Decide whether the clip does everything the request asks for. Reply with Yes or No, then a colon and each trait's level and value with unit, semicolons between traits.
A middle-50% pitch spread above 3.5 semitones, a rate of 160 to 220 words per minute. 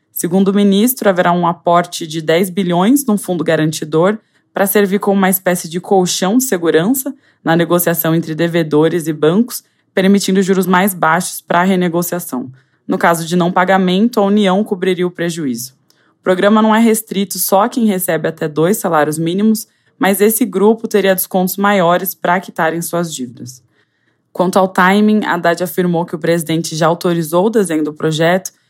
No: average, 3.2 semitones; average, 170 wpm